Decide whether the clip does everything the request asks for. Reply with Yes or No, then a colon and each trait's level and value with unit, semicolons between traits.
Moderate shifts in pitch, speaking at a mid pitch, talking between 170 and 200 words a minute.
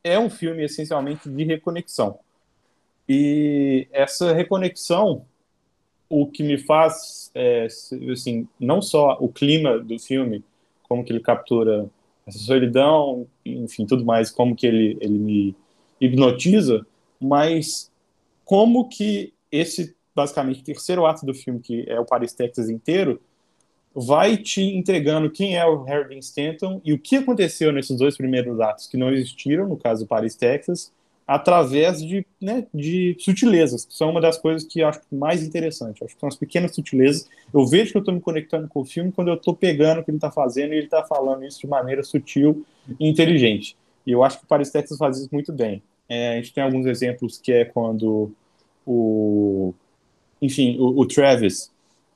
Yes: average, 4.8 semitones; medium, 145 Hz; average, 175 wpm